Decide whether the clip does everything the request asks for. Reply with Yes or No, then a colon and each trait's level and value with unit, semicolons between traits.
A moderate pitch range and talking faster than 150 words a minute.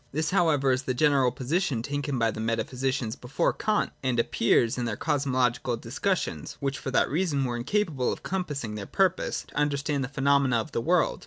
Yes: average, 3.4 semitones; average, 195 wpm